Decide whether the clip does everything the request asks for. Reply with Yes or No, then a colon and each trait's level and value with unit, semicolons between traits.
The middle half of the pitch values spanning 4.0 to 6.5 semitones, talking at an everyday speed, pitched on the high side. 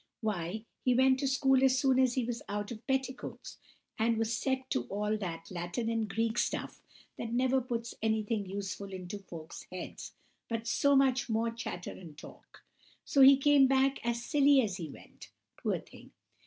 Yes: average, 4.5 semitones; average, 180 wpm; high, 230 Hz